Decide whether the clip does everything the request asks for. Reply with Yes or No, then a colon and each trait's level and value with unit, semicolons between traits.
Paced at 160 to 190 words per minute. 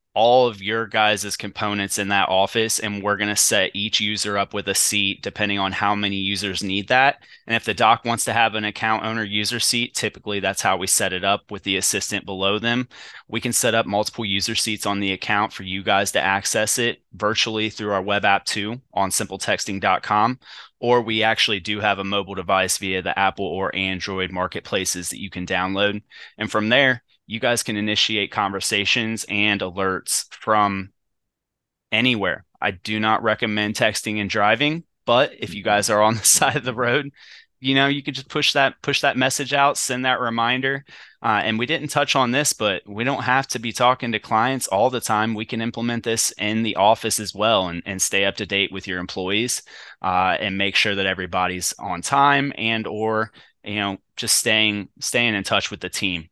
No: fast, 205 wpm